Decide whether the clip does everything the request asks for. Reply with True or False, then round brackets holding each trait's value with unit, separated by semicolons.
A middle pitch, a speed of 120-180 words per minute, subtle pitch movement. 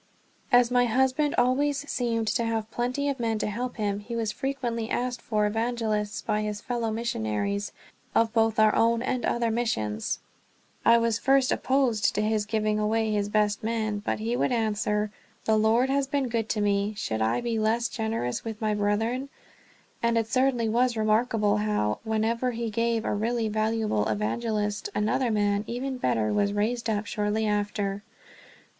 False (225 Hz; 175 wpm; 2.3 semitones)